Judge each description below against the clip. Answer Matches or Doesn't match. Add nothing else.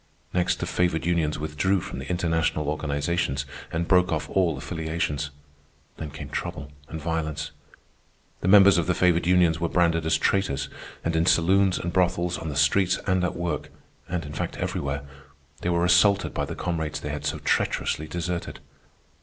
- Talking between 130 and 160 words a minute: Doesn't match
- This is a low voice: Matches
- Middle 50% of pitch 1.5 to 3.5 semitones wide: Matches